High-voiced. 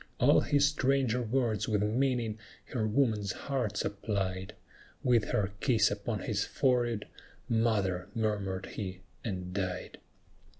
No: low, 110 Hz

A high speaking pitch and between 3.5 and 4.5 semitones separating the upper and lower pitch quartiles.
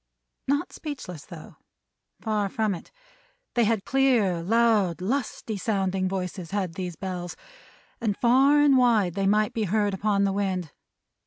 Yes: high, 205 Hz; average, 3.8 semitones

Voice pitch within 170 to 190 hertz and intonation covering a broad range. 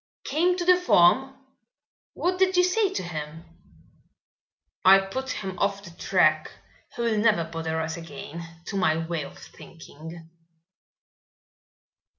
Yes: medium, 185 Hz; wide, 8.5 semitones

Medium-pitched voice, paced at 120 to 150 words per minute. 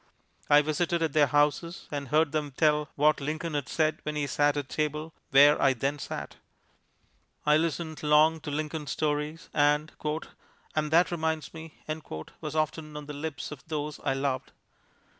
No: medium, 150 Hz; average, 165 wpm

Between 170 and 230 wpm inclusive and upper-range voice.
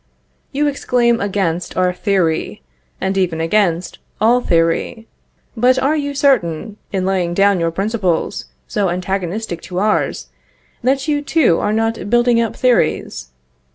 No: slow, 135 wpm; high, 200 Hz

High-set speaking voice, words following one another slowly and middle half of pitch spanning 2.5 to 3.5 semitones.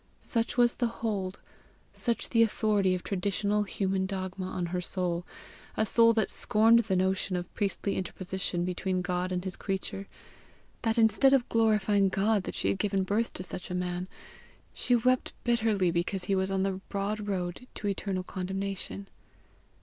No: high, 195 Hz; average, 165 wpm; average, 2.8 semitones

